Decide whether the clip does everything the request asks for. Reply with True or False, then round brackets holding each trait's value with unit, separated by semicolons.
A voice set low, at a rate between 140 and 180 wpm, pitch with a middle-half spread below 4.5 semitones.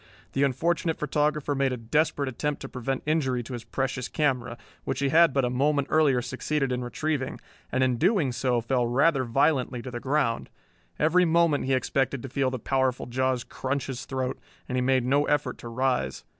False (130 Hz; 195 wpm; 2.7 semitones)